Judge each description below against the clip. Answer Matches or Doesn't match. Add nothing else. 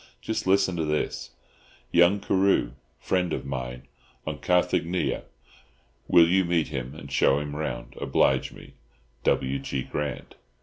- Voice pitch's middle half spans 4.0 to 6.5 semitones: Matches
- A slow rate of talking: Matches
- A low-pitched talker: Matches